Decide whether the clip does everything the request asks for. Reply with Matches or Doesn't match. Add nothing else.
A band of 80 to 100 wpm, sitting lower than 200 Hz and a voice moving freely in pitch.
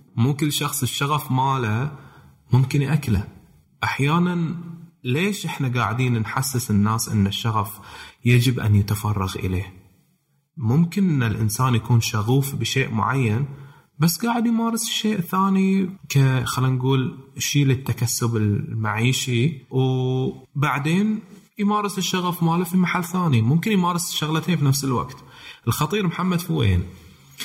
Doesn't match